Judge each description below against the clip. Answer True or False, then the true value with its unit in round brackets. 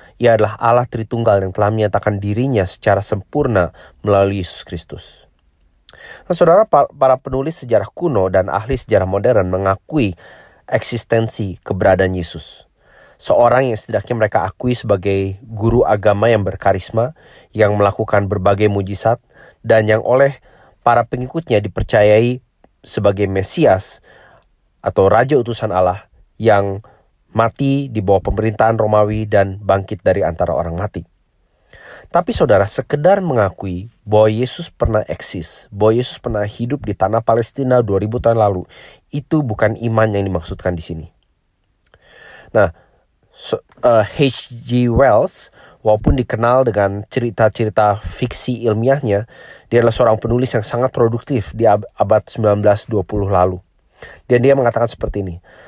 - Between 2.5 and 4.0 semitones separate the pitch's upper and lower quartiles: True (3.5 semitones)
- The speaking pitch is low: True (110 Hz)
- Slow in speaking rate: True (125 wpm)